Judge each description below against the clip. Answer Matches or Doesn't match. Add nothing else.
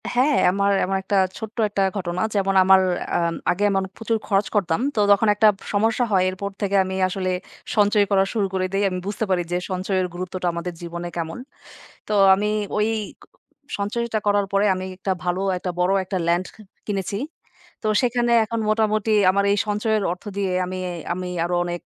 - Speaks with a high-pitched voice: Matches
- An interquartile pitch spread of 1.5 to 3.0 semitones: Matches